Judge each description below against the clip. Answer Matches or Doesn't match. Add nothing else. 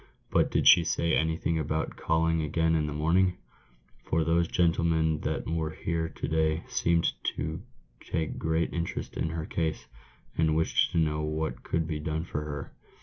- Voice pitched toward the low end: Matches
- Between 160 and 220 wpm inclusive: Matches